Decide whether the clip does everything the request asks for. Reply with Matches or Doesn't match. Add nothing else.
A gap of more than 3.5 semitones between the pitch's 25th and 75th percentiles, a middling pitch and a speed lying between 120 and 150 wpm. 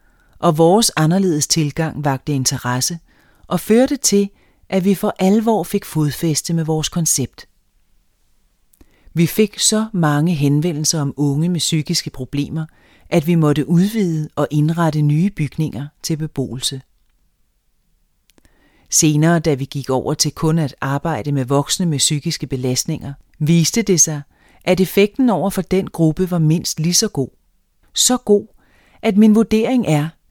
Matches